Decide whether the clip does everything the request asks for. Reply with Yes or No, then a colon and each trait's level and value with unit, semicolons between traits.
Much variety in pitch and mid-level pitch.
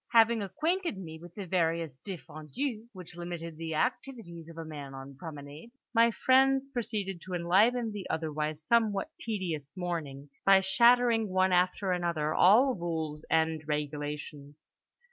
Yes: wide, 5.9 semitones; medium, 175 Hz